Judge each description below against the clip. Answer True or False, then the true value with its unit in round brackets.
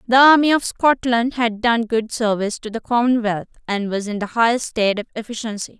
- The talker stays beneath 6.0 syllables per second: True (5.6 syllables/s)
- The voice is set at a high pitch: True (230 Hz)